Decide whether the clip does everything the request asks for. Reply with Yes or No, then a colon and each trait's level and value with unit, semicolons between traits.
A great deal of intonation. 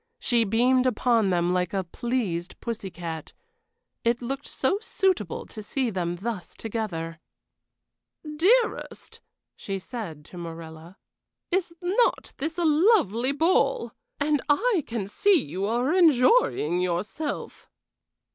Yes: wide, 8.9 semitones